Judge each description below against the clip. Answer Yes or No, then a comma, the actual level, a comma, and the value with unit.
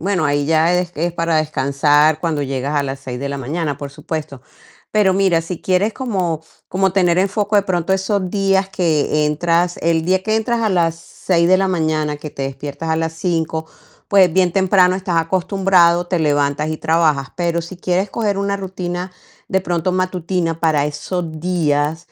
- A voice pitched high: No, medium, 170 Hz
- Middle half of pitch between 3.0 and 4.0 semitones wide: Yes, average, 3.3 semitones